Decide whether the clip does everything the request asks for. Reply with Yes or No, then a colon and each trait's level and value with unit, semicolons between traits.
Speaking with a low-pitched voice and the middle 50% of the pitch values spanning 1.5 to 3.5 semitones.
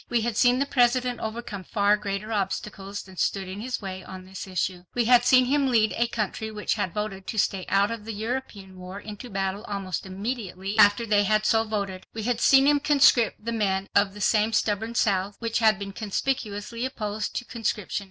No: high, 210 Hz; average, 3.0 semitones